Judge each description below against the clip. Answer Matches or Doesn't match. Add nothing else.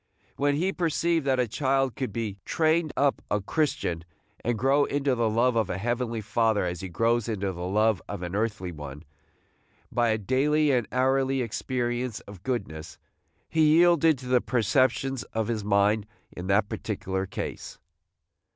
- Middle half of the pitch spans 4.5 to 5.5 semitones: Matches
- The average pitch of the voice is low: Matches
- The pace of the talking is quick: Doesn't match